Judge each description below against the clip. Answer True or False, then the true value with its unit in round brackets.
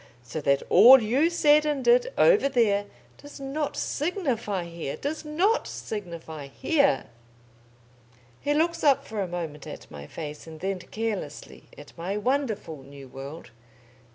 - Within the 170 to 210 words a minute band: False (145 wpm)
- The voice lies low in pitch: False (210 Hz)